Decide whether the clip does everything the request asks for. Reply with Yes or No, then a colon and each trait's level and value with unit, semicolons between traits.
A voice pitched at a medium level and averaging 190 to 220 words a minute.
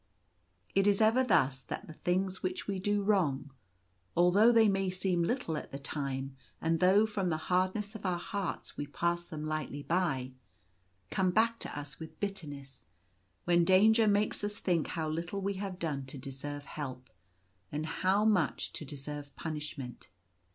No: medium, 170 Hz; average, 170 wpm